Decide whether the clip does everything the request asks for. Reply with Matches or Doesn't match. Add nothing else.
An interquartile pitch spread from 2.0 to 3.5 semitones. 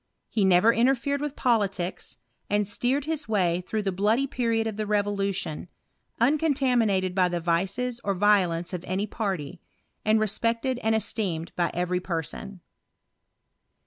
Doesn't match